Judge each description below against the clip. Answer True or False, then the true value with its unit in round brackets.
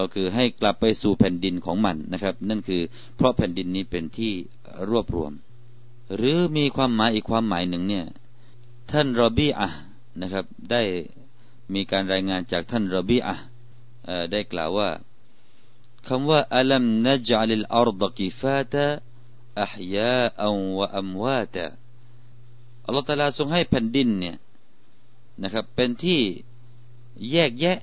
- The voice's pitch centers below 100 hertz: False (120 Hz)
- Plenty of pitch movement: False (4.2 semitones)